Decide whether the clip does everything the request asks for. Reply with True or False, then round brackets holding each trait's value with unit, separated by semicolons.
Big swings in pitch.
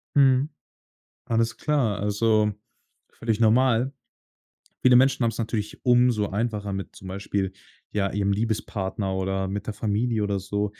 False (2.8 semitones)